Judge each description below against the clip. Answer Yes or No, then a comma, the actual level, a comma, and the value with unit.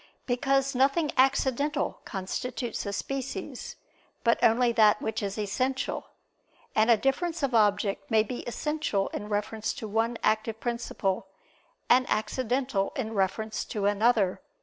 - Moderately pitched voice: No, high, 230 Hz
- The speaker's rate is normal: No, slow, 130 wpm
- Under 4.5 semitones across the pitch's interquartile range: Yes, average, 3.9 semitones